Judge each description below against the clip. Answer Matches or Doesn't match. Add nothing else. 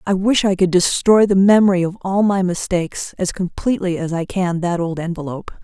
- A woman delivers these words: Matches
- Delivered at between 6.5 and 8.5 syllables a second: Doesn't match